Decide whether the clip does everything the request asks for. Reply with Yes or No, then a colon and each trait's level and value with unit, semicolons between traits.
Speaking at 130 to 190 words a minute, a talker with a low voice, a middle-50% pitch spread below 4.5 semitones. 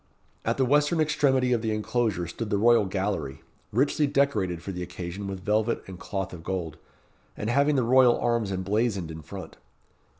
No: average, 175 wpm; low, 105 Hz; average, 5.2 semitones